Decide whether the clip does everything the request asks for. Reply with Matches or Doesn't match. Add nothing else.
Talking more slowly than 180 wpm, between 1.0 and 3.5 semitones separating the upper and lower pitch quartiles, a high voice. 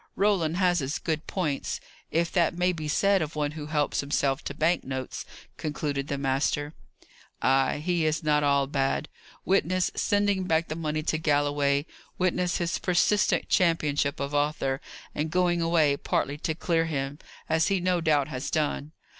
Doesn't match